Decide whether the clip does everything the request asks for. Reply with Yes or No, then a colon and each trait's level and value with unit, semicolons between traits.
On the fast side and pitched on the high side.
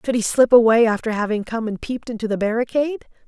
Yes: fast, 220 wpm; high, 230 Hz